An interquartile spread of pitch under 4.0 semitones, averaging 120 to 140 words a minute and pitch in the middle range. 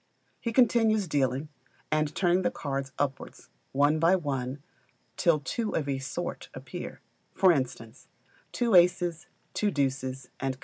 No: average, 4.9 semitones; slow, 135 wpm; medium, 150 Hz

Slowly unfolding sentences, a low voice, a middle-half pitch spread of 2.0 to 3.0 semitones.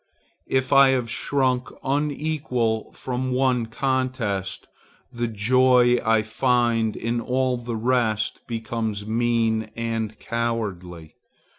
Yes: slow, 105 wpm; low, 120 Hz; narrow, 2.5 semitones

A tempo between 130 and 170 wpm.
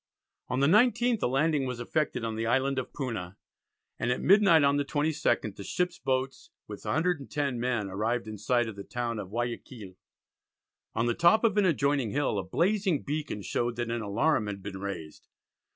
No: average, 185 wpm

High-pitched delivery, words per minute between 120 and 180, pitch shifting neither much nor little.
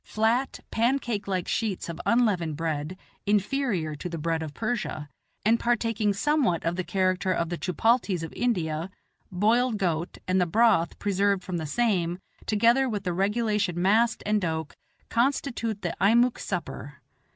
Yes: high, 200 Hz; average, 150 wpm; average, 5.0 semitones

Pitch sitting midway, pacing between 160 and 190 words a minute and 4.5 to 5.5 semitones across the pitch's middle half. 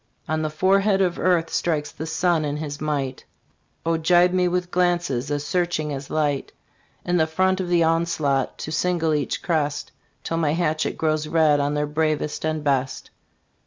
No: medium, 155 Hz; average, 175 wpm; average, 2.9 semitones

